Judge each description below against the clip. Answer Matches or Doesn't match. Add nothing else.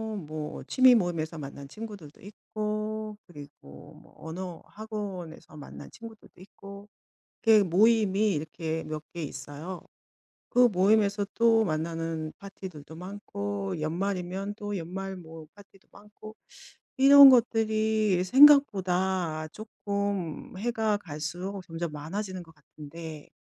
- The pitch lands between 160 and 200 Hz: Matches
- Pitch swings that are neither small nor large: Matches